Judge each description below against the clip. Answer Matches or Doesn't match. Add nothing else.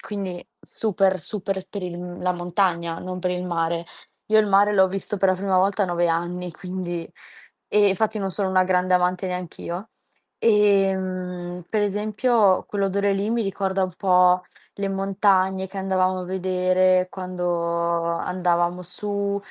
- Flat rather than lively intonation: Matches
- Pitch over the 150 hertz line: Matches